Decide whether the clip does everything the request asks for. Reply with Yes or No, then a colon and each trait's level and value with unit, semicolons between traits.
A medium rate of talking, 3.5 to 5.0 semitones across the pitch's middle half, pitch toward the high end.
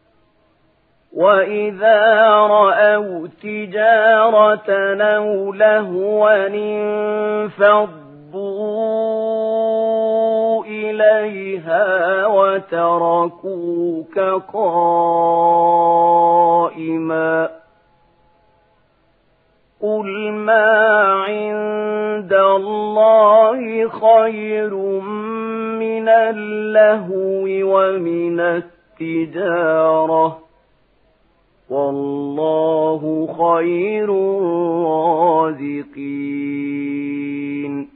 No: slow, 30 wpm; average, 4.0 semitones; high, 195 Hz